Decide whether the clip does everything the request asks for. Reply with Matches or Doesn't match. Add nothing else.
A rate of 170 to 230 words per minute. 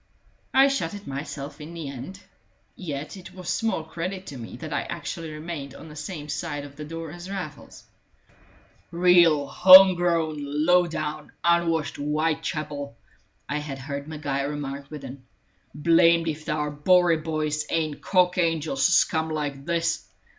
Doesn't match